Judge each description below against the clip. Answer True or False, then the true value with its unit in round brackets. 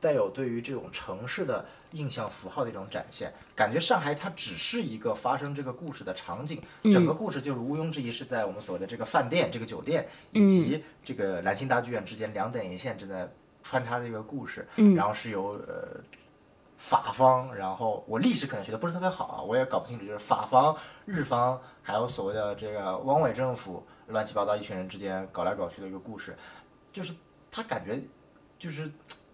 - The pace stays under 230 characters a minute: False (315 characters per minute)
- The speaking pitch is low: True (130 Hz)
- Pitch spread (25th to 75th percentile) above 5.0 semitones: True (5.6 semitones)